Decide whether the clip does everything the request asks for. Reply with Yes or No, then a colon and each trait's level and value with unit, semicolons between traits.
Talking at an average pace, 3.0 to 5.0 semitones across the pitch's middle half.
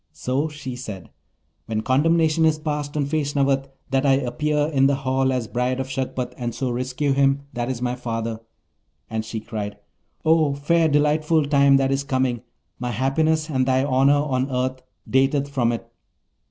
No: average, 170 wpm; narrow, 2.5 semitones